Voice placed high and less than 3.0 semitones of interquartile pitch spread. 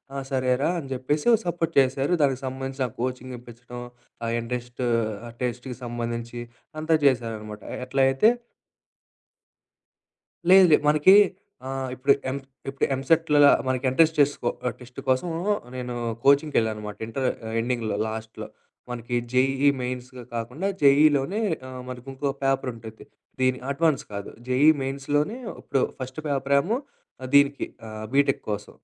No: low, 130 Hz; narrow, 2.5 semitones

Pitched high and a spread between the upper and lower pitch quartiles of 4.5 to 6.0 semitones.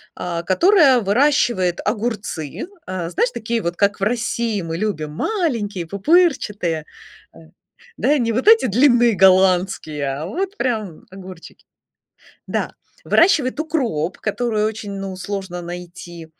Yes: high, 205 Hz; wide, 5.5 semitones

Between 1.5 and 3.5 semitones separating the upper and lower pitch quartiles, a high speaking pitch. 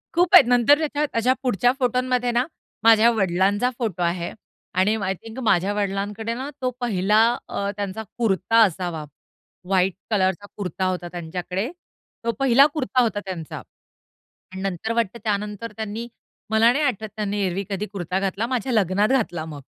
No: average, 3.9 semitones; high, 210 Hz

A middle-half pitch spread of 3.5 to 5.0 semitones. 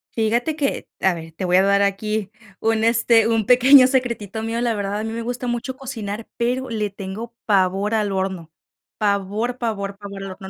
No: average, 3.1 semitones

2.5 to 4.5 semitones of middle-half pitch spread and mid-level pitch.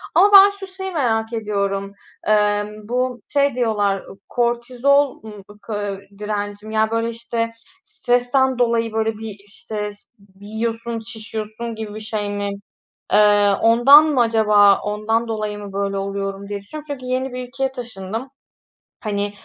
No: average, 2.8 semitones; high, 220 Hz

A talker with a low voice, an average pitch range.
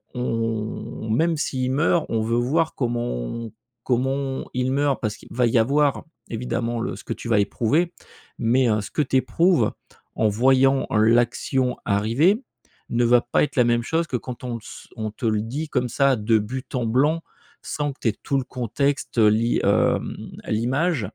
Yes: low, 125 Hz; average, 3.3 semitones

